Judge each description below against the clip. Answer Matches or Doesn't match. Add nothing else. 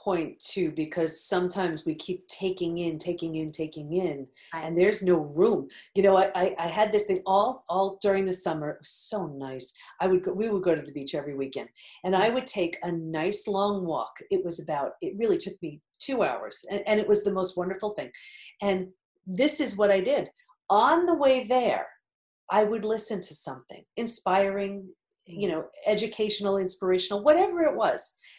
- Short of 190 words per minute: Doesn't match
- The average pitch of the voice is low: Doesn't match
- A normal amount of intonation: Matches